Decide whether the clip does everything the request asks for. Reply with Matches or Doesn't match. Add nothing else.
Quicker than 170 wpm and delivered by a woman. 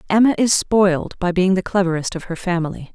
Matches